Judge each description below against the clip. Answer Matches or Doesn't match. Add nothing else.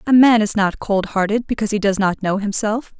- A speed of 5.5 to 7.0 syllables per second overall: Matches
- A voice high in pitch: Matches